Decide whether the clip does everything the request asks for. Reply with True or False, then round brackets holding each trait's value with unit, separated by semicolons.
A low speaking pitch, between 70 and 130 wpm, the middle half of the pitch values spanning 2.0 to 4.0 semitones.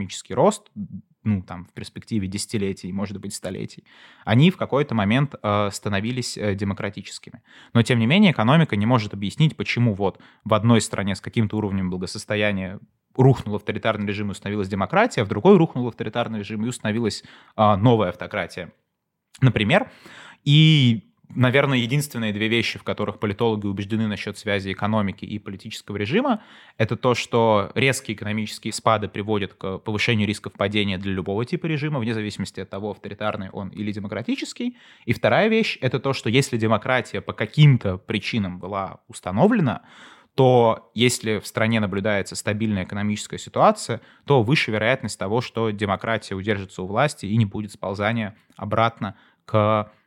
False (110 Hz; 150 wpm; 3.1 semitones)